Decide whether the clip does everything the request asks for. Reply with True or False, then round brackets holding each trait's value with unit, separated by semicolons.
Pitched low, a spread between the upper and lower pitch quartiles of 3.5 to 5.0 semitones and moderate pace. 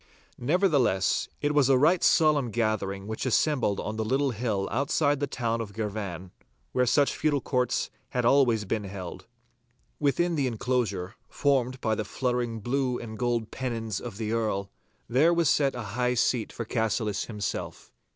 True (120 Hz; 4.0 semitones; 160 wpm)